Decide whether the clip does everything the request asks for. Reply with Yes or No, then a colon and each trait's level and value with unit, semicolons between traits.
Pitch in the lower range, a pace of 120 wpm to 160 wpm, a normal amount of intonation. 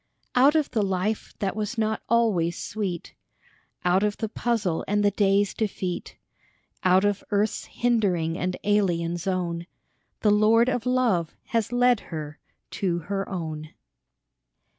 No: high, 200 Hz; average, 140 wpm; average, 3.8 semitones